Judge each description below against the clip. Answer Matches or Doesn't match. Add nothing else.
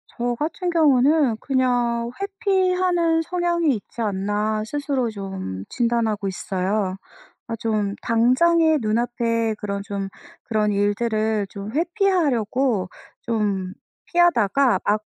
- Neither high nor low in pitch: Doesn't match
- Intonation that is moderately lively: Doesn't match